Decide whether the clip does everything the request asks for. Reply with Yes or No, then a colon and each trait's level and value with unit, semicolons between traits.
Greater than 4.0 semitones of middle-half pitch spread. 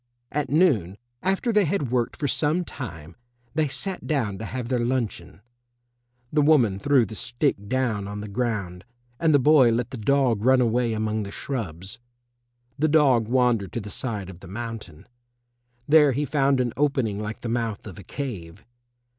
Yes: average, 5.3 semitones